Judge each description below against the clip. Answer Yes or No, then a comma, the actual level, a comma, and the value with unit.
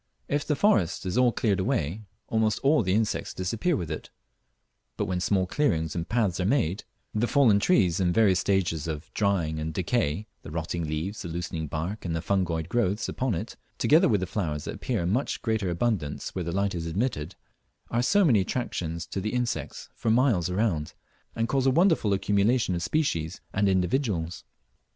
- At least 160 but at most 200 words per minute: Yes, average, 190 wpm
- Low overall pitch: Yes, very low, 95 Hz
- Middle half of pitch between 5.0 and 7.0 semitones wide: Yes, wide, 5.5 semitones